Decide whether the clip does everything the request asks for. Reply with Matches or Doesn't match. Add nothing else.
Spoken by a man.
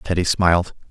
Matches